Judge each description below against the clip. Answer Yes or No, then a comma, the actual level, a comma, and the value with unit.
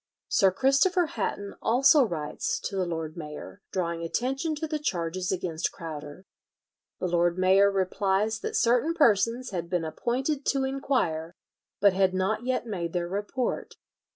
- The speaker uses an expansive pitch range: Yes, wide, 6.7 semitones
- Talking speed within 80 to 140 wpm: No, average, 150 wpm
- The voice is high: Yes, high, 195 Hz